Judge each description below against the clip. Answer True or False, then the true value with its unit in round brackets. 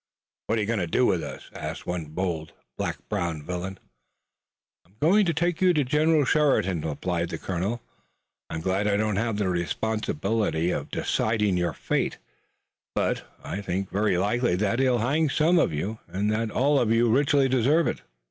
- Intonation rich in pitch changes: True (6.5 semitones)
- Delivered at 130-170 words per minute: False (185 wpm)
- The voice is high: False (105 Hz)